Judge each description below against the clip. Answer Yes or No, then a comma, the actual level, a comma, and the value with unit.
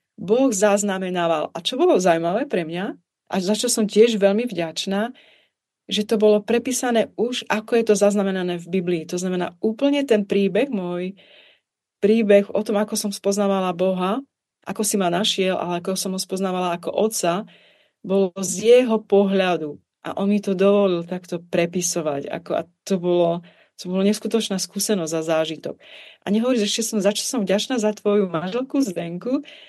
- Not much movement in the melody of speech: No, average, 3.2 semitones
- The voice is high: Yes, high, 200 Hz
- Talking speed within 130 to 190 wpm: Yes, fast, 170 wpm